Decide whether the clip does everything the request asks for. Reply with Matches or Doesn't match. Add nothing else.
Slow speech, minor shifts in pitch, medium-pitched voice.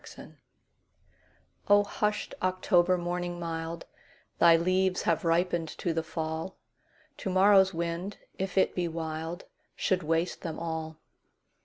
Matches